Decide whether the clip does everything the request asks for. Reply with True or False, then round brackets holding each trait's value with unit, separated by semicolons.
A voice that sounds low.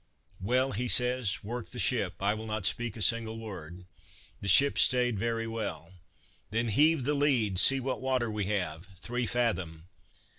True (115 Hz)